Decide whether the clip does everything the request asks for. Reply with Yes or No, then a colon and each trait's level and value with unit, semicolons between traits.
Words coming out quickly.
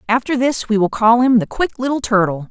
Yes: fast, 240 wpm